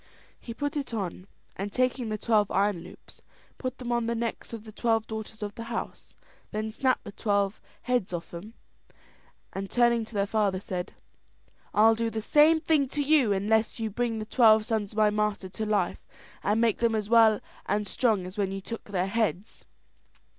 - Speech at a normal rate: Yes, average, 195 wpm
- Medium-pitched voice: No, high, 220 Hz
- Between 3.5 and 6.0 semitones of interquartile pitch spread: No, narrow, 2.4 semitones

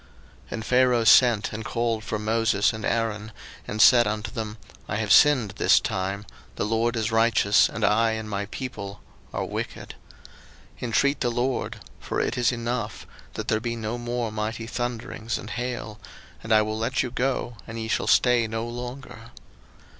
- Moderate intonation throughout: No, narrow, 2.0 semitones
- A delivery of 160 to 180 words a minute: Yes, average, 175 wpm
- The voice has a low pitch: Yes, low, 115 Hz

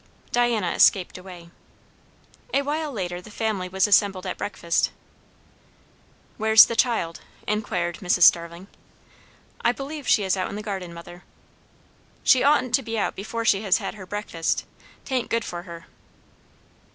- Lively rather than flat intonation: No, average, 4.3 semitones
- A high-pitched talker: Yes, high, 200 Hz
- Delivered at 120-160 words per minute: Yes, average, 150 wpm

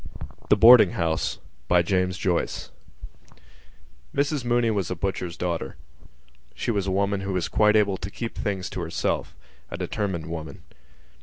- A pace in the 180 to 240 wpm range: No, slow, 135 wpm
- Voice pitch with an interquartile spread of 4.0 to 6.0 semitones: No, average, 2.9 semitones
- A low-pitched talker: Yes, very low, 95 Hz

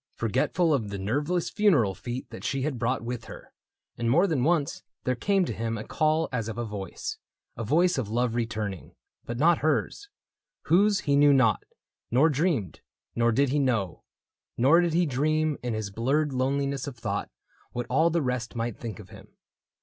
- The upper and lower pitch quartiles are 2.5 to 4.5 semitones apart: No, average, 5.2 semitones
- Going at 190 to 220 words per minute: Yes, average, 195 wpm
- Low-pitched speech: Yes, low, 130 Hz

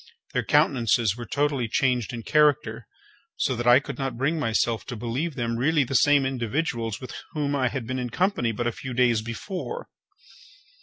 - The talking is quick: No, average, 185 wpm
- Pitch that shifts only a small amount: No, average, 3.7 semitones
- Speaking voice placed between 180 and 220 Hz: No, low, 130 Hz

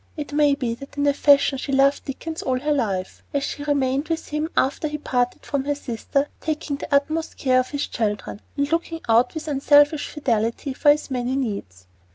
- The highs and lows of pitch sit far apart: No, narrow, 2.6 semitones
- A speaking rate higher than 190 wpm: Yes, fast, 205 wpm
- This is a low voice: No, very high, 280 Hz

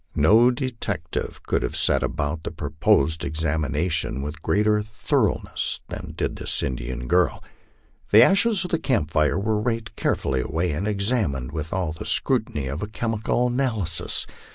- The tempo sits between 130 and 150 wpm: No, average, 160 wpm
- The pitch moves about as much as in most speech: No, wide, 6.8 semitones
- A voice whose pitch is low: Yes, very low, 95 Hz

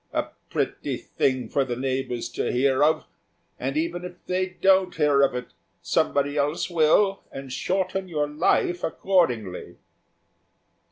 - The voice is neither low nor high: Yes, medium, 150 Hz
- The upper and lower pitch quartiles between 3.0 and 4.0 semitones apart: No, average, 5.1 semitones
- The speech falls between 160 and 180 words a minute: No, slow, 135 wpm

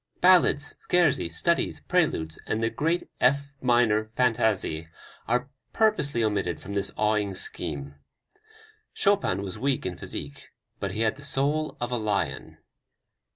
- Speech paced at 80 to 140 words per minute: Yes, slow, 135 wpm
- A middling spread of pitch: No, wide, 6.4 semitones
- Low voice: Yes, low, 115 Hz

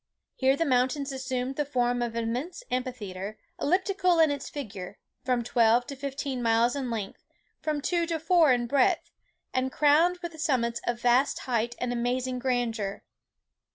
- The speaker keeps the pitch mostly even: No, average, 3.3 semitones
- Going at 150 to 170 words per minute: Yes, average, 160 wpm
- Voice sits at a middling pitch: No, very high, 255 Hz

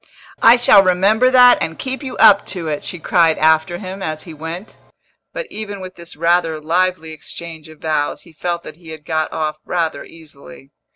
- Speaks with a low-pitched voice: No, medium, 170 Hz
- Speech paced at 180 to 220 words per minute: Yes, average, 190 wpm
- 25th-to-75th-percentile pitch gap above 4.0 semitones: No, average, 3.1 semitones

